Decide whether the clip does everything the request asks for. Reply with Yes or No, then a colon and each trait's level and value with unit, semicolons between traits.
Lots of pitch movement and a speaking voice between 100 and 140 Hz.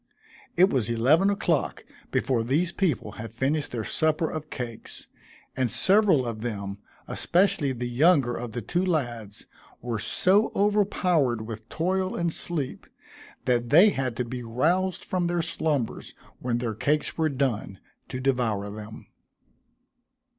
Yes: wide, 6.6 semitones; low, 135 Hz